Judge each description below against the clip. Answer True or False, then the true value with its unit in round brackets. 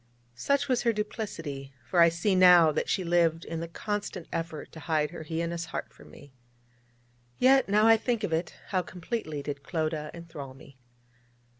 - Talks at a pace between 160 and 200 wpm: True (175 wpm)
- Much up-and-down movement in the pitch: False (4.5 semitones)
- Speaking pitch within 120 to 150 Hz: False (170 Hz)